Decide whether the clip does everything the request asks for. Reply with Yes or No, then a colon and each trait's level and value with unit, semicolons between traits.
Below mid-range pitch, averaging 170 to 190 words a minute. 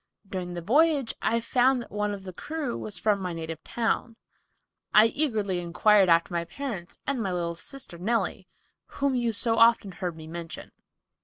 No: high, 210 Hz; average, 175 wpm